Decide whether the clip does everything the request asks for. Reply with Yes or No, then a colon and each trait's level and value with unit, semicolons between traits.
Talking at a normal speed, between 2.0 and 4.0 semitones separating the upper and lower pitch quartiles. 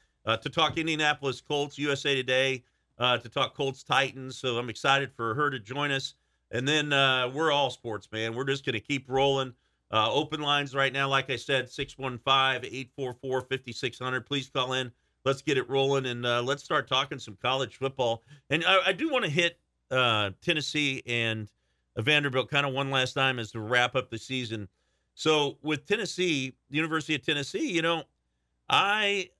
Yes: average, 185 wpm; average, 2.8 semitones